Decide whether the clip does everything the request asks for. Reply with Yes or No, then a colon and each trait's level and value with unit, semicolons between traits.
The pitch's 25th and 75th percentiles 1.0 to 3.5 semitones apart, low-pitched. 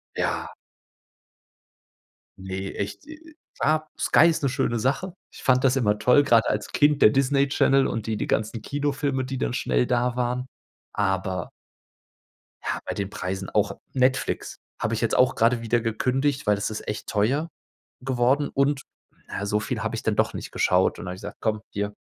No: average, 4.7 semitones; low, 120 Hz